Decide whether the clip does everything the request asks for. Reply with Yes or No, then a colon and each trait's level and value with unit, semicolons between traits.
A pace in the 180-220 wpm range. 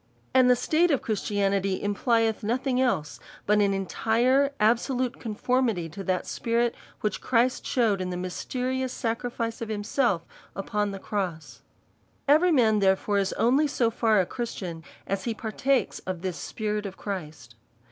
No: average, 150 wpm